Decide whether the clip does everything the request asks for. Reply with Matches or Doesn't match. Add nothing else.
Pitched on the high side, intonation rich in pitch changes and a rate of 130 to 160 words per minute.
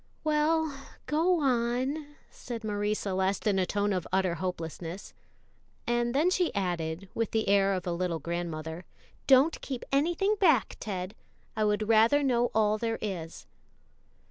Matches